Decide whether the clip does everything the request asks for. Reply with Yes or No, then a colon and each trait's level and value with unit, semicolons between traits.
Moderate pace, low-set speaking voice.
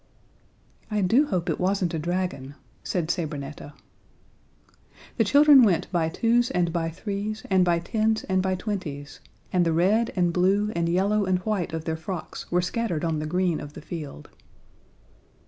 No: average, 165 wpm; medium, 180 Hz